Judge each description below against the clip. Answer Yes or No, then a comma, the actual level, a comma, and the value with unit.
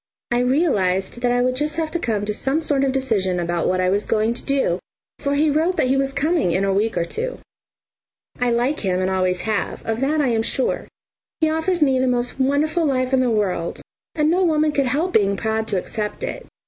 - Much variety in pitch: Yes, wide, 6.3 semitones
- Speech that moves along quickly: Yes, fast, 230 wpm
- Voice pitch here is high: Yes, very high, 255 Hz